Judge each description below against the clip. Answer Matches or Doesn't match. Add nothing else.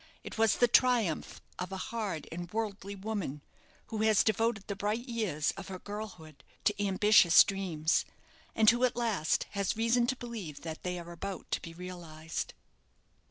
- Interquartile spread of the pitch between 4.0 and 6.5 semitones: Matches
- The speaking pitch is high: Matches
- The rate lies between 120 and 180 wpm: Matches